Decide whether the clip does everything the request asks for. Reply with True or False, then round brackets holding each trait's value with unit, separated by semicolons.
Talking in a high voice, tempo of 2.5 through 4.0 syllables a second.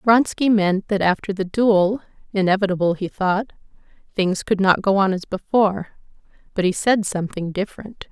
False (195 Hz; 5.1 syllables/s)